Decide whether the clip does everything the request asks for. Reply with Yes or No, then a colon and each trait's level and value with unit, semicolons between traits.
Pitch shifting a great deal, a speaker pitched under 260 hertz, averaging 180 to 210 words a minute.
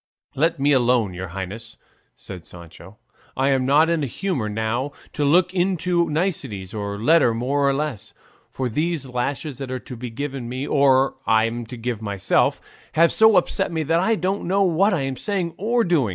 Yes: wide, 6.7 semitones; low, 135 Hz; average, 185 wpm